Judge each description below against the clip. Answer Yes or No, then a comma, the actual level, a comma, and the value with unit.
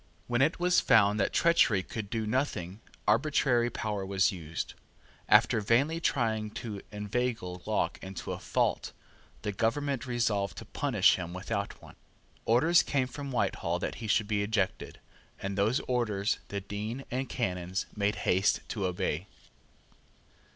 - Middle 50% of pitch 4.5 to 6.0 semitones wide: No, average, 3.8 semitones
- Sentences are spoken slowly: No, average, 145 wpm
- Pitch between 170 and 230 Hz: No, low, 105 Hz